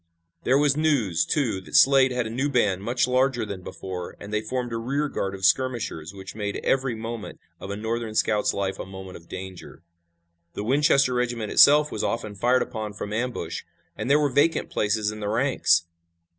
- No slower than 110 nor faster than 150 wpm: No, average, 195 wpm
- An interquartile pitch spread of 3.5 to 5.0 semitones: Yes, average, 4.5 semitones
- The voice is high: No, low, 115 Hz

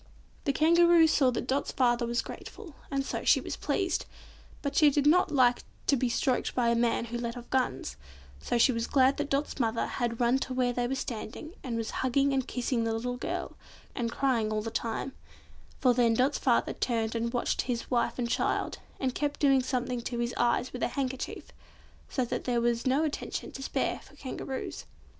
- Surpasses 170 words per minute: Yes, fast, 205 wpm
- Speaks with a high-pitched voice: Yes, very high, 250 Hz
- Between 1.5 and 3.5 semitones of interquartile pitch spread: Yes, narrow, 2.5 semitones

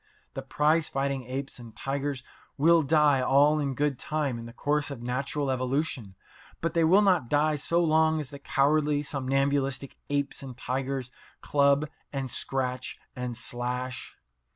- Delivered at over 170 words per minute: No, average, 155 wpm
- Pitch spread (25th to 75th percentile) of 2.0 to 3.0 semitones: Yes, narrow, 2.6 semitones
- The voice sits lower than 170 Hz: Yes, medium, 140 Hz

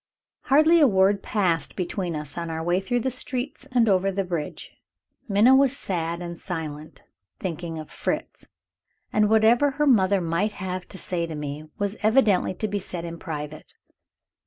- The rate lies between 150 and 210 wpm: Yes, average, 170 wpm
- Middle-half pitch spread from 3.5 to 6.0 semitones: Yes, average, 4.7 semitones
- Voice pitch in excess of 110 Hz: Yes, high, 190 Hz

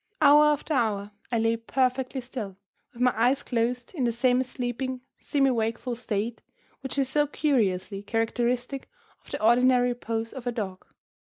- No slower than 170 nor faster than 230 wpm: No, average, 160 wpm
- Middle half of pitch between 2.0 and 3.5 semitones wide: Yes, narrow, 2.4 semitones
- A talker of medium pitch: No, high, 245 Hz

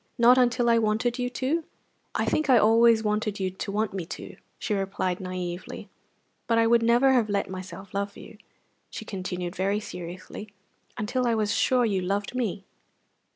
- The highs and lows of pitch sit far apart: No, average, 3.6 semitones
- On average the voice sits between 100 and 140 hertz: No, high, 215 Hz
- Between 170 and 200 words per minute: Yes, average, 175 wpm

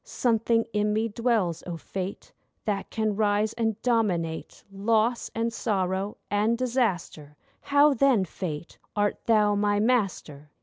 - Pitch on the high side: Yes, high, 210 Hz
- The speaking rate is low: Yes, slow, 130 wpm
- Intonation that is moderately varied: Yes, average, 3.1 semitones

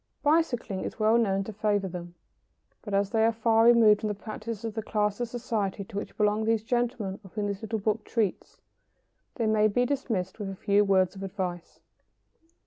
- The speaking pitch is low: No, high, 210 Hz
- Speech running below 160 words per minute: No, average, 200 wpm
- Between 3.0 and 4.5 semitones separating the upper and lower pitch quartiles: No, narrow, 2.4 semitones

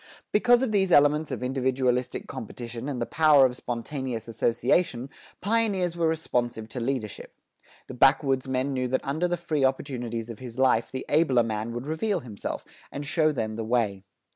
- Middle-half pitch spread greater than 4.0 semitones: Yes, average, 4.6 semitones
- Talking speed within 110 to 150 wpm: No, average, 165 wpm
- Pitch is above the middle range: No, low, 130 Hz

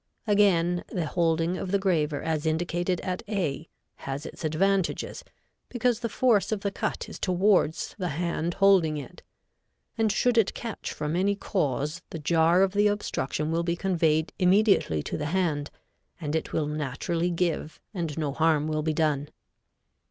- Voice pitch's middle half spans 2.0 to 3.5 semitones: No, average, 3.9 semitones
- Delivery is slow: No, average, 165 wpm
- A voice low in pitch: No, medium, 170 Hz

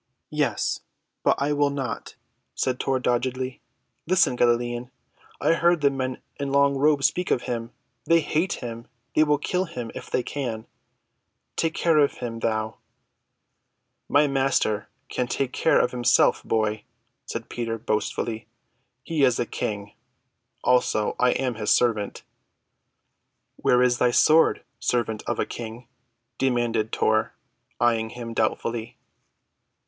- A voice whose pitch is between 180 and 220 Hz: No, low, 125 Hz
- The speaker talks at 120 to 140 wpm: Yes, slow, 135 wpm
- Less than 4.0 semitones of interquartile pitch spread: Yes, average, 3.5 semitones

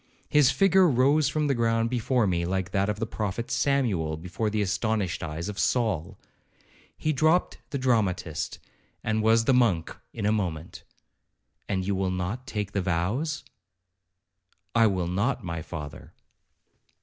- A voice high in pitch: No, low, 105 Hz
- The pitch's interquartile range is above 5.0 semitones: Yes, wide, 5.4 semitones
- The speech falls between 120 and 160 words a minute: Yes, average, 150 wpm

